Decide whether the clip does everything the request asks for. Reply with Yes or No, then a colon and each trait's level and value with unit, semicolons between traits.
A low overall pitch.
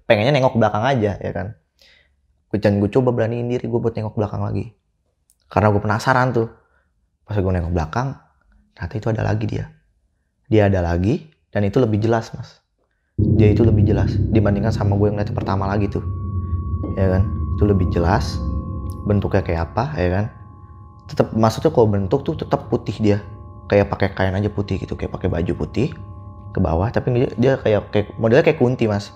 Yes: low, 105 Hz